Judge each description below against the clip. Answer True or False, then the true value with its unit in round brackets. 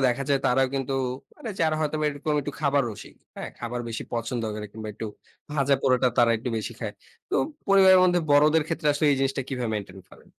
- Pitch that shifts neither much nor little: True (4.1 semitones)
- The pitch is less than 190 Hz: True (135 Hz)